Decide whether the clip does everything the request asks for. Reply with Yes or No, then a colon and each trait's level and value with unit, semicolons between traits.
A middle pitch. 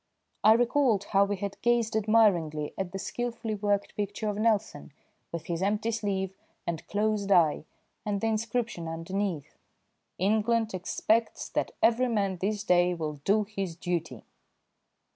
No: high, 205 Hz